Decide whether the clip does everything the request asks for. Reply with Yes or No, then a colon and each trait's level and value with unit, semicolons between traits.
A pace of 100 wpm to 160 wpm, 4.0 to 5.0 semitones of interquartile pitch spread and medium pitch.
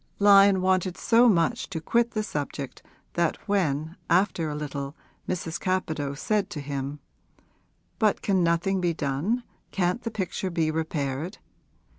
Yes: average, 140 wpm; average, 4.7 semitones; medium, 175 Hz